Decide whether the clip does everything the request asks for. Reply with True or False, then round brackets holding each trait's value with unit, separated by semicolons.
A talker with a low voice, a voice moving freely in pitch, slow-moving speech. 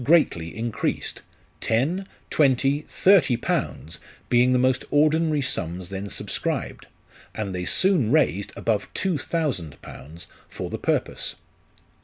True (125 Hz; 8.1 semitones; 120 wpm)